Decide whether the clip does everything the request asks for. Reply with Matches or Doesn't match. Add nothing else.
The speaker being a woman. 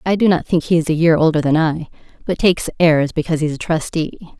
Matches